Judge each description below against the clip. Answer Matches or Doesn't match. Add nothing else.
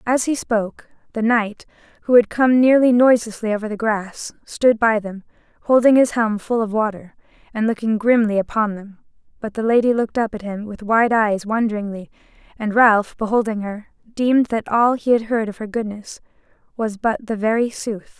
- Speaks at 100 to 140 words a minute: Doesn't match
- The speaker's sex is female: Matches